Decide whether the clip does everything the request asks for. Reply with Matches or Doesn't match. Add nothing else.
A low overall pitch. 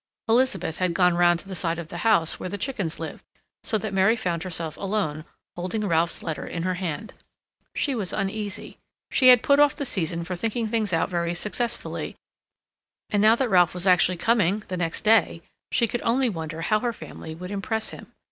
Doesn't match